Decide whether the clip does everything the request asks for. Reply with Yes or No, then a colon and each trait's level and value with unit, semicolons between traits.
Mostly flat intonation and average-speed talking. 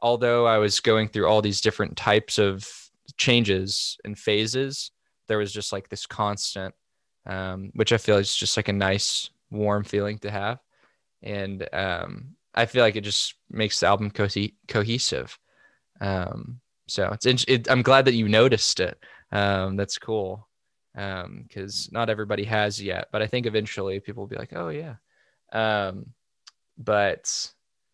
Yes: narrow, 2.0 semitones; average, 160 wpm